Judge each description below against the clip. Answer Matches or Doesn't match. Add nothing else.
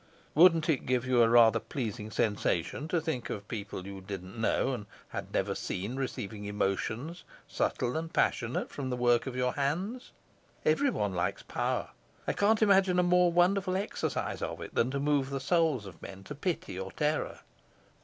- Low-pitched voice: Matches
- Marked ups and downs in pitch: Matches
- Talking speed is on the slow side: Doesn't match